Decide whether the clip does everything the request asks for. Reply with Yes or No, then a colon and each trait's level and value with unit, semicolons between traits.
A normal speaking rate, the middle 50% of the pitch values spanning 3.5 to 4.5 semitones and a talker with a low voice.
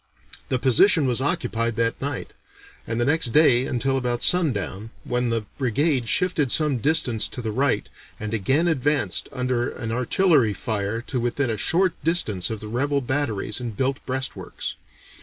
Yes: average, 160 wpm; average, 3.9 semitones; low, 125 Hz